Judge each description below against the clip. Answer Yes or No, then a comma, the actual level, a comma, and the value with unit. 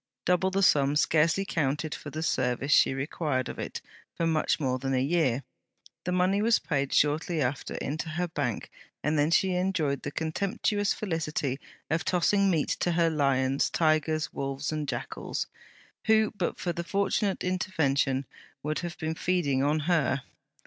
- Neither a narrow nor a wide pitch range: Yes, average, 4.2 semitones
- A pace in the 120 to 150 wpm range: No, average, 165 wpm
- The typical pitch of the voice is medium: Yes, medium, 155 Hz